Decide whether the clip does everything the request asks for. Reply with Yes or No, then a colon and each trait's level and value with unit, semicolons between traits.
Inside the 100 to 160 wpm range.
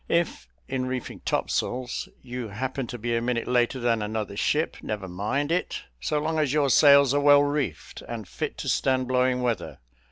No: average, 185 wpm